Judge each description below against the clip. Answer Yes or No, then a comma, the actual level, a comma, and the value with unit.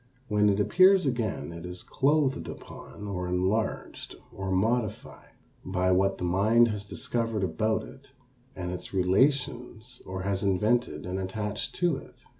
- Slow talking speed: No, average, 145 wpm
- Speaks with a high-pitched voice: No, low, 105 Hz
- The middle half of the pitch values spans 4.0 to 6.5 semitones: Yes, average, 4.4 semitones